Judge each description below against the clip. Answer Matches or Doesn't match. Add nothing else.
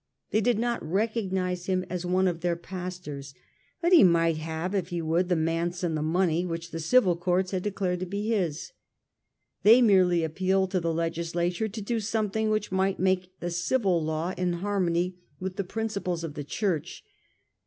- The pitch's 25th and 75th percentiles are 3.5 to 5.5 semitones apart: Doesn't match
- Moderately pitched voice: Matches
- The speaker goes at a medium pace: Matches